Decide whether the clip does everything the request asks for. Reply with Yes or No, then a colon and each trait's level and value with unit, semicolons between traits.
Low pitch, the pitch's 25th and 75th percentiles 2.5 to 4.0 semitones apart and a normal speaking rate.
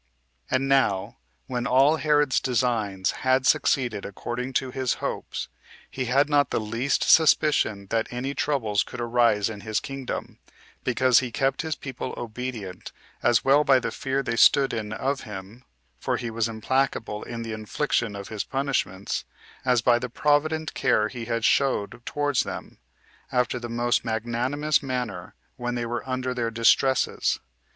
Yes: low, 125 Hz; average, 3.0 semitones; average, 160 wpm